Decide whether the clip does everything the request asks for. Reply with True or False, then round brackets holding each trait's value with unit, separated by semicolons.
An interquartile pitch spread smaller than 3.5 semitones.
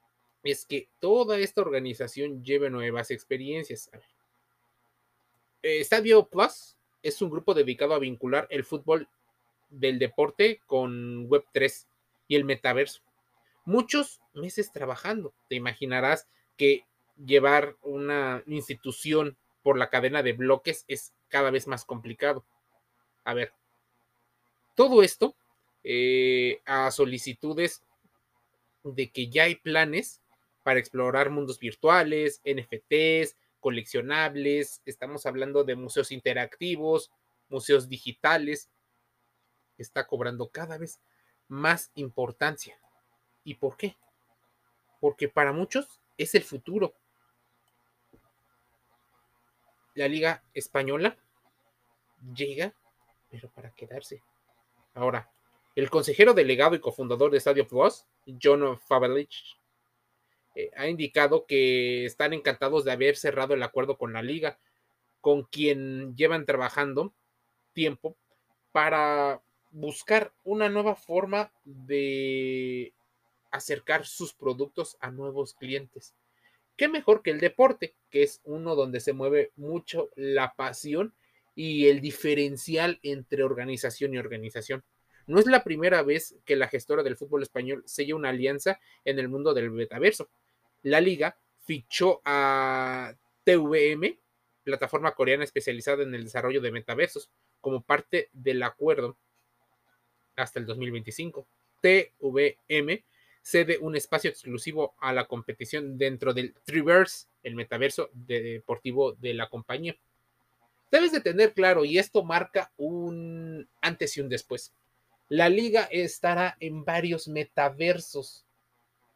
False (4.4 semitones)